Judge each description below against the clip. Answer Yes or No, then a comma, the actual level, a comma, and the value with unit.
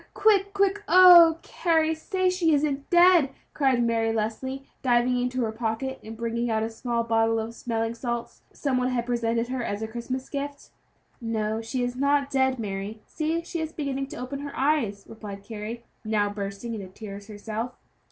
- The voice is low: No, high, 240 Hz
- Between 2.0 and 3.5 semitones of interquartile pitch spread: No, average, 4.0 semitones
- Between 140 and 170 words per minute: No, average, 180 wpm